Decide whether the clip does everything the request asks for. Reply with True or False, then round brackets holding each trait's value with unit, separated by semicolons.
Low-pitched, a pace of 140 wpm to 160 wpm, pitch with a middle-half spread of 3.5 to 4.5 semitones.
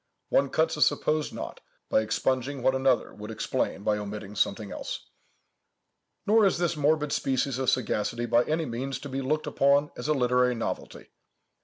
False (130 Hz; 170 wpm; 4.0 semitones)